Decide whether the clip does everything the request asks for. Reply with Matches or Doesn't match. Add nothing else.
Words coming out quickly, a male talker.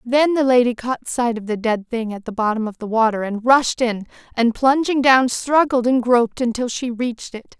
Doesn't match